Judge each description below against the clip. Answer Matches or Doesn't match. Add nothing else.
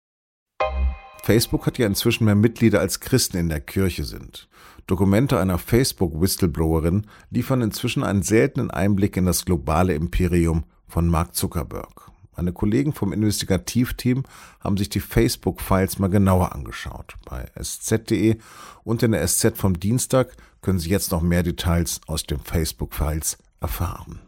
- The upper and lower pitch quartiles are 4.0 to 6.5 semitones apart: Matches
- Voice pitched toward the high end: Doesn't match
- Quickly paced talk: Doesn't match